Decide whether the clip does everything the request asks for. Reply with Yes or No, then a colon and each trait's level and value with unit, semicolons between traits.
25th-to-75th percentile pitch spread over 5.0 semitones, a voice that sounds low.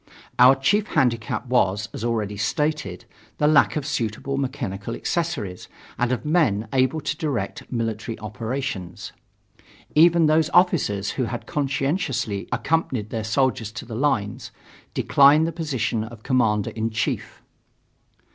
Yes: wide, 5.4 semitones; low, 125 Hz